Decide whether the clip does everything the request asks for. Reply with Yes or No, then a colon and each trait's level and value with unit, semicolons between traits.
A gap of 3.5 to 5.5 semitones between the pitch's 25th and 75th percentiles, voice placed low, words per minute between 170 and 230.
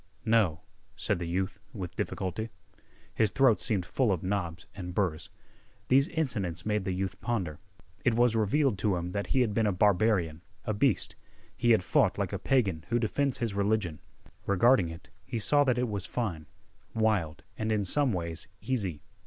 Yes: average, 4.5 semitones; low, 100 Hz; average, 180 wpm